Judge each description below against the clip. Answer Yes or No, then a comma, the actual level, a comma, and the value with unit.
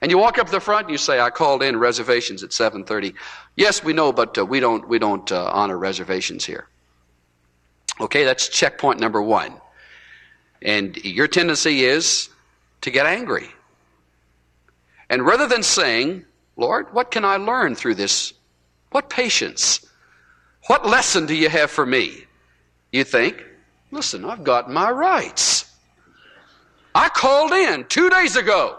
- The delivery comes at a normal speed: Yes, average, 150 wpm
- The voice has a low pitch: No, medium, 150 Hz